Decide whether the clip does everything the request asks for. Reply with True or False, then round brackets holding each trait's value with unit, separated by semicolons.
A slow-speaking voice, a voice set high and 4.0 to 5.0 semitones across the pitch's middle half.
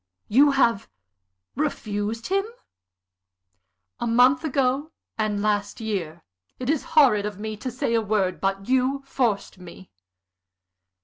True (125 wpm; 230 Hz; 4.5 semitones)